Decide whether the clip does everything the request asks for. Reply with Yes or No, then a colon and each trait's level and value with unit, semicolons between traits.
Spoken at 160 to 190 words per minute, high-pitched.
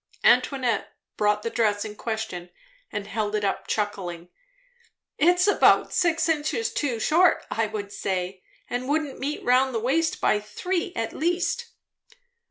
No: average, 145 wpm; high, 230 Hz